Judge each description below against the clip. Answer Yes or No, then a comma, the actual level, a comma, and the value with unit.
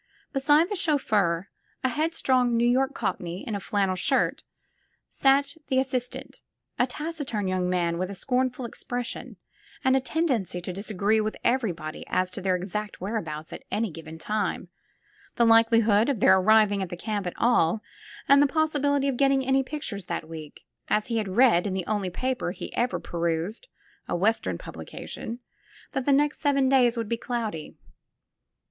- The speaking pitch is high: Yes, high, 225 Hz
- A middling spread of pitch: No, wide, 6.0 semitones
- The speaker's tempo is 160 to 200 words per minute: Yes, average, 165 wpm